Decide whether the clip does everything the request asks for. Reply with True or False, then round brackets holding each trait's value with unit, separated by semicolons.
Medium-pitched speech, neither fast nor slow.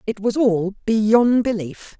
False (215 Hz; 150 wpm)